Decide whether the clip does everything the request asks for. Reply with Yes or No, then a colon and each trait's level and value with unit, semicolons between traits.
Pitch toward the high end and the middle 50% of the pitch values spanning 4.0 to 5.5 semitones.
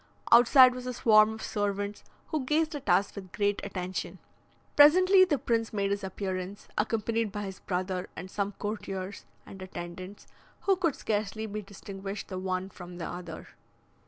No: high, 205 Hz; average, 3.4 semitones